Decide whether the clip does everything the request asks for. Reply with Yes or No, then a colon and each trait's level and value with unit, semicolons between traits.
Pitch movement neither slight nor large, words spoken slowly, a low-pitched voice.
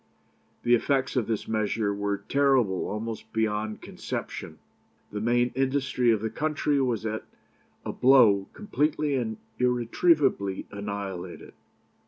Yes: average, 4.3 semitones; slow, 120 wpm; low, 115 Hz